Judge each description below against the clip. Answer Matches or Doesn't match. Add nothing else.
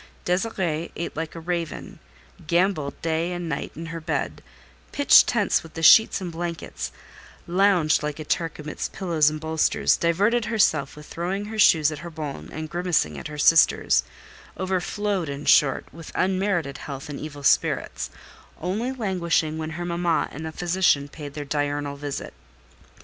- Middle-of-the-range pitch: Matches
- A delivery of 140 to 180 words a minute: Matches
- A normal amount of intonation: Matches